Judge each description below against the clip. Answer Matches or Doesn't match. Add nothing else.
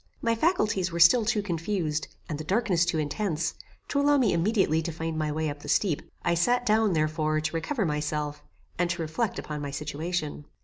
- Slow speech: Doesn't match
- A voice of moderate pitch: Matches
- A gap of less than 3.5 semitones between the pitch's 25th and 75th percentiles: Doesn't match